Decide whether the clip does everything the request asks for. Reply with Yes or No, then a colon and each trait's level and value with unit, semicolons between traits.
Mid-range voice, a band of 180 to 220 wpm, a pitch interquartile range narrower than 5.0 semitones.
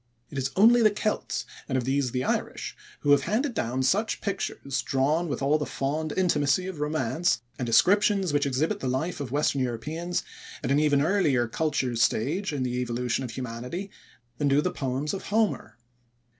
No: medium, 145 Hz; average, 185 wpm; wide, 5.5 semitones